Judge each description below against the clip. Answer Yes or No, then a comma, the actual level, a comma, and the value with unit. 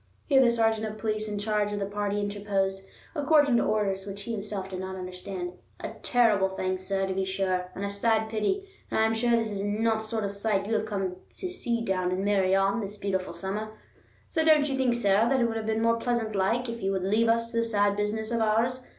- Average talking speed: No, fast, 240 wpm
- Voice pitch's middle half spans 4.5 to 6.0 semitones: No, average, 2.9 semitones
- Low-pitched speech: No, high, 210 Hz